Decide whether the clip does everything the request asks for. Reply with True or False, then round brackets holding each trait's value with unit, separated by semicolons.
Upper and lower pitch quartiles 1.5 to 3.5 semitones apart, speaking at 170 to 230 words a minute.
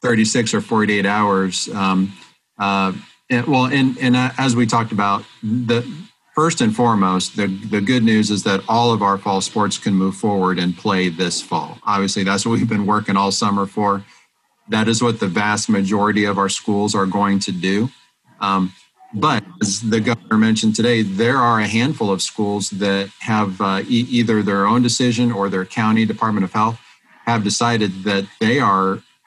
True (3.0 semitones; 185 wpm)